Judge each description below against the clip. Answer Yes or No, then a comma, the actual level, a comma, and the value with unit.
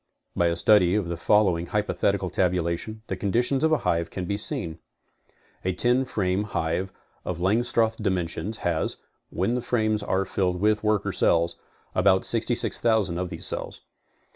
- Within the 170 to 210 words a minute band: No, average, 150 wpm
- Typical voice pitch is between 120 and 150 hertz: No, low, 100 Hz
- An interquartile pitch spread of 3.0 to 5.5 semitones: Yes, average, 3.5 semitones